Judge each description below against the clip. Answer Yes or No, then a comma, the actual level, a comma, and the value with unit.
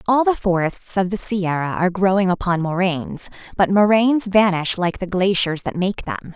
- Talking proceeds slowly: No, average, 180 wpm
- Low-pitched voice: No, high, 190 Hz